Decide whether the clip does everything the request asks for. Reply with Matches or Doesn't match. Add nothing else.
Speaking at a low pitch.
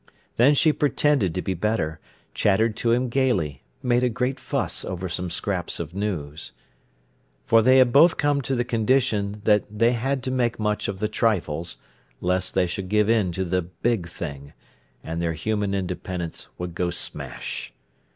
Matches